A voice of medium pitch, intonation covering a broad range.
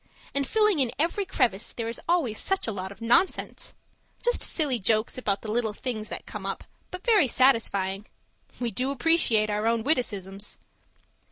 No: high, 235 Hz; wide, 5.9 semitones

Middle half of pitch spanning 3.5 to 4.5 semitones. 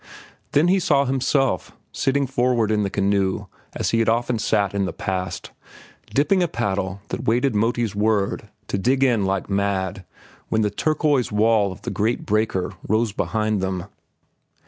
Yes: average, 4.0 semitones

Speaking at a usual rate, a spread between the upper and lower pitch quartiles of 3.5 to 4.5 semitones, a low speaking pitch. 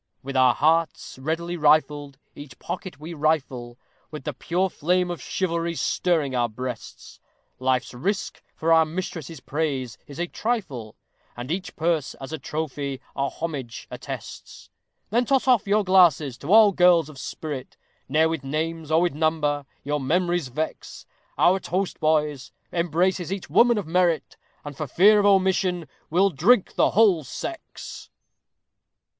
No: average, 150 wpm; average, 4.2 semitones; medium, 160 Hz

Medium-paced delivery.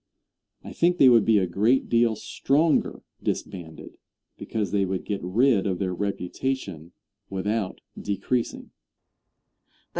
No: slow, 120 wpm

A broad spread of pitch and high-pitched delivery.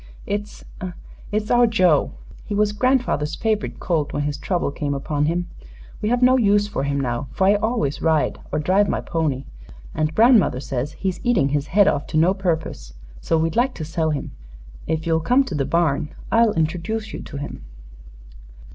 No: wide, 6.1 semitones; medium, 165 Hz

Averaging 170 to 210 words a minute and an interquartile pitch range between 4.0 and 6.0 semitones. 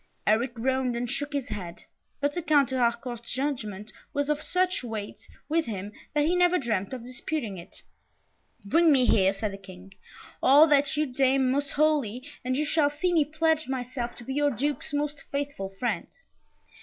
Yes: average, 180 wpm; average, 4.3 semitones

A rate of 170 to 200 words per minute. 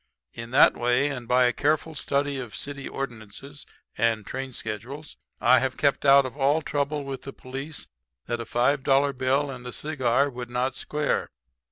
Yes: average, 180 wpm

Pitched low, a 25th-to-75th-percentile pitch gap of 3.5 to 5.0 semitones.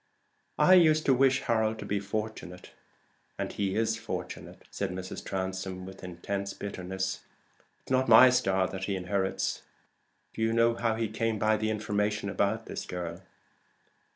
No: low, 105 Hz; average, 3.0 semitones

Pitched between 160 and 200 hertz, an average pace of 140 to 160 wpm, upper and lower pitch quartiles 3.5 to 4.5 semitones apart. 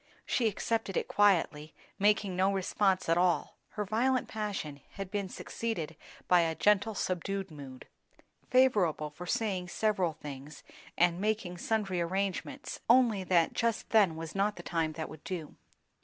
Yes: high, 190 Hz; average, 150 wpm; average, 4.1 semitones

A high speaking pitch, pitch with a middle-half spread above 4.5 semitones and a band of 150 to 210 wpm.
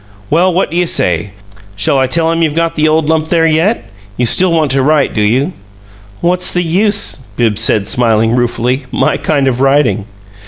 No: medium, 150 Hz; wide, 5.4 semitones; average, 195 wpm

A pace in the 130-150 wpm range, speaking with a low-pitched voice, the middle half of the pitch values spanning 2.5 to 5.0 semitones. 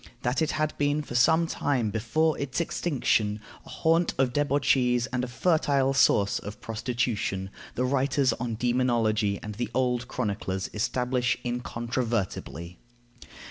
Yes: slow, 135 wpm; low, 125 Hz; average, 3.7 semitones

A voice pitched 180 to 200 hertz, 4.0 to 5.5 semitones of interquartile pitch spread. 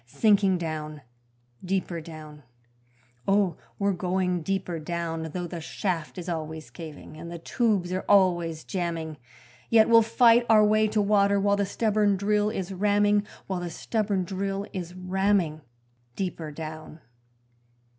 No: medium, 185 Hz; average, 3.6 semitones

